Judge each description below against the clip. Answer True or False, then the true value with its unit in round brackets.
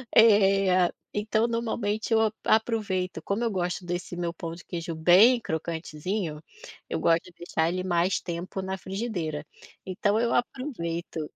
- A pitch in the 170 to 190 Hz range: True (185 Hz)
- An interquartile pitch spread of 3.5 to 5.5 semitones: True (4.2 semitones)